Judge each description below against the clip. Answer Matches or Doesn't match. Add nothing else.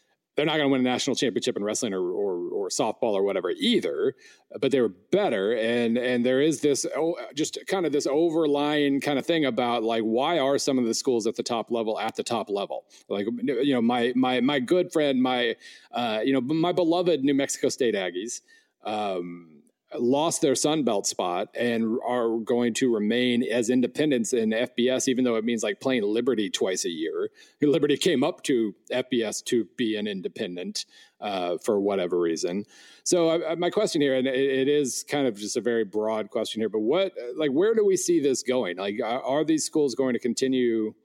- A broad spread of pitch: Matches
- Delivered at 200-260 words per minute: Matches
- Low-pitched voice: Matches